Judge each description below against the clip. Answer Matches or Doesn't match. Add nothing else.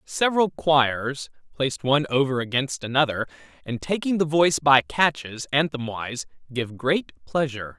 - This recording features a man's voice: Matches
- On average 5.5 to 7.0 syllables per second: Doesn't match